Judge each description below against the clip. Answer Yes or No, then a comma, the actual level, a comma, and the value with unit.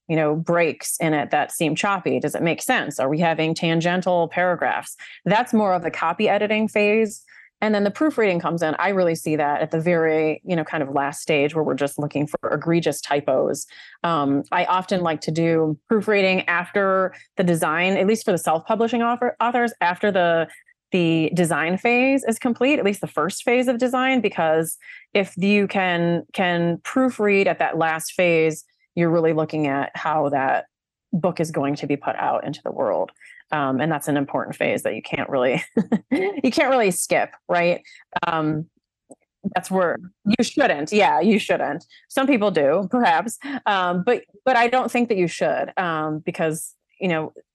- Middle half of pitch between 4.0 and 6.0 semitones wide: Yes, average, 4.8 semitones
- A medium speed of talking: Yes, average, 185 wpm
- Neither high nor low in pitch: Yes, medium, 175 Hz